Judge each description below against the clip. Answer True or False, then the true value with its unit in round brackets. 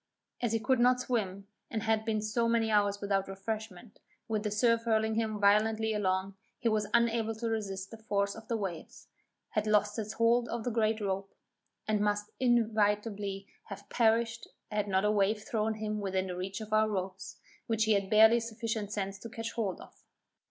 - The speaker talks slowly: False (190 wpm)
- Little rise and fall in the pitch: True (2.0 semitones)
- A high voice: True (215 Hz)